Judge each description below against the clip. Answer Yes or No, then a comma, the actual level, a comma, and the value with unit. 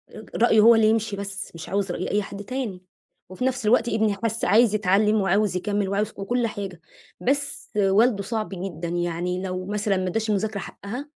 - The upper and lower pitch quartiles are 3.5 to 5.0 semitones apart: No, narrow, 2.6 semitones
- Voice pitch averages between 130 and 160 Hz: No, high, 205 Hz